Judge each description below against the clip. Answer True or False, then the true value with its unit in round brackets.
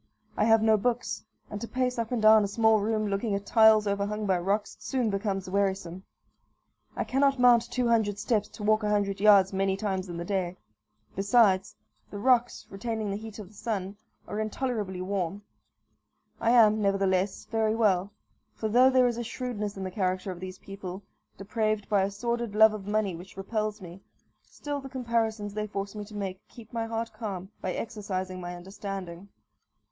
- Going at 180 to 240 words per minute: True (185 wpm)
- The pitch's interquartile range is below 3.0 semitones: True (2.5 semitones)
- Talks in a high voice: True (210 Hz)